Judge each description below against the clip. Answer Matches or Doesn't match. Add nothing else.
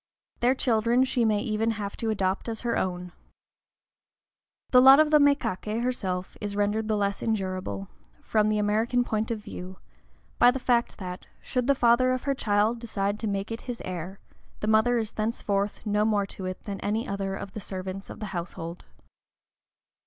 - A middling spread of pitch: Matches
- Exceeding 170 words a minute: Matches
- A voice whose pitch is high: Matches